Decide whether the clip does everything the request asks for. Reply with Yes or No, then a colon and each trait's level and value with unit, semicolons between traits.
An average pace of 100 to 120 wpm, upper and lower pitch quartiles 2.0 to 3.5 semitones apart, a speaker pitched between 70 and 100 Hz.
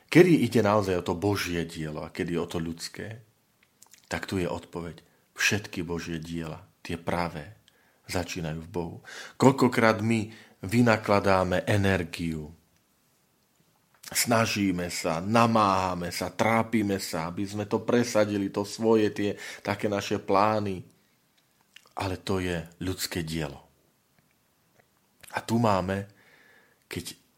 No: average, 115 wpm; average, 3.9 semitones; very low, 95 Hz